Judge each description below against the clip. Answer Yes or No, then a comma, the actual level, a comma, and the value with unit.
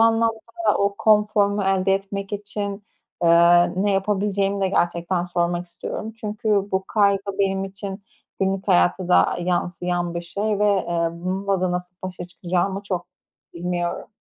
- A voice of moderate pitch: No, high, 195 Hz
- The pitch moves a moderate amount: No, narrow, 2.3 semitones